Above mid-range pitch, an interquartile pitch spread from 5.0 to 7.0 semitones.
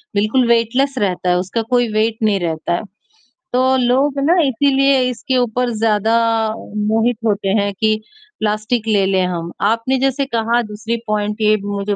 No: high, 220 Hz; average, 3.4 semitones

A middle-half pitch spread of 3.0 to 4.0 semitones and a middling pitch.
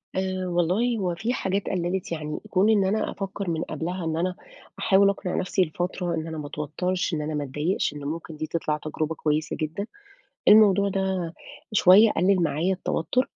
Yes: average, 3.3 semitones; medium, 180 Hz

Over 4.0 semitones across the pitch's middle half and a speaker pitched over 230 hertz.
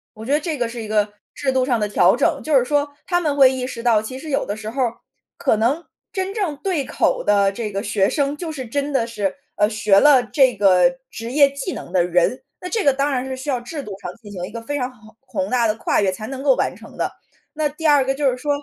Yes: average, 5.0 semitones; very high, 255 Hz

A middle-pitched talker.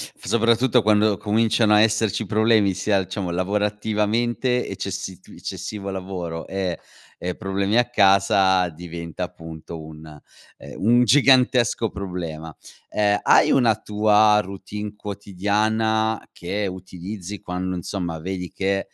No: low, 100 Hz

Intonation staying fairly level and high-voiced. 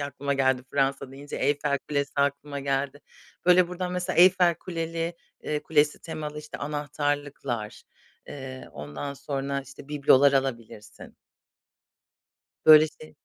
No: narrow, 2.0 semitones; medium, 145 Hz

